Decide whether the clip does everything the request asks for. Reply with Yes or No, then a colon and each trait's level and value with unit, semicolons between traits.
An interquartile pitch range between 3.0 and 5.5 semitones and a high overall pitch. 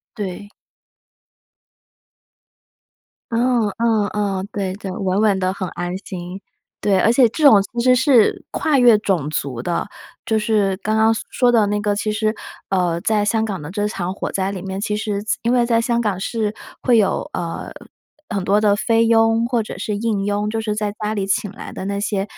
No: narrow, 2.5 semitones; high, 210 Hz